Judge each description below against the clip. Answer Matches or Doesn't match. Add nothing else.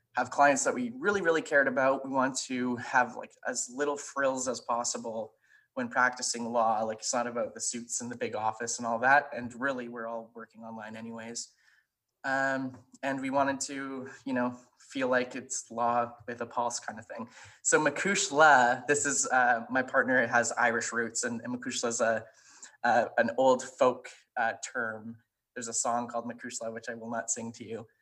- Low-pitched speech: Matches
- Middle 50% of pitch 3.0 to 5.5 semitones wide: Doesn't match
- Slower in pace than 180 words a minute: Doesn't match